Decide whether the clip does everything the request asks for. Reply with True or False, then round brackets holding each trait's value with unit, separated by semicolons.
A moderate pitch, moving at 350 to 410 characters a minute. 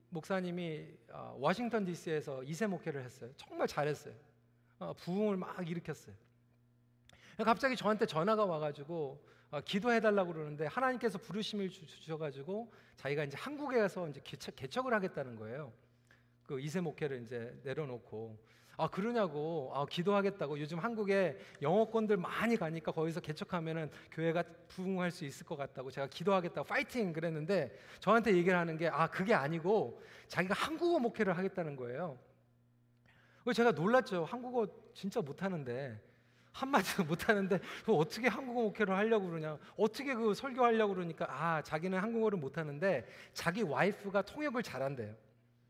True (175 Hz; 360 characters per minute)